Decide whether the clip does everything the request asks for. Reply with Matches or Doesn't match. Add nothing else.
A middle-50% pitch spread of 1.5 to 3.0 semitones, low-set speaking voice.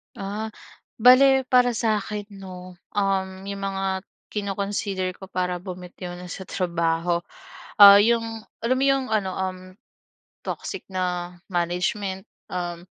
Doesn't match